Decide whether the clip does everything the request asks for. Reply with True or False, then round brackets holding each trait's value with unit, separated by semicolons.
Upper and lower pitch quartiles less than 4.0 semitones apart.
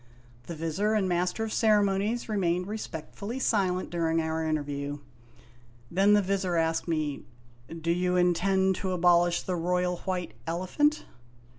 True (3.0 semitones)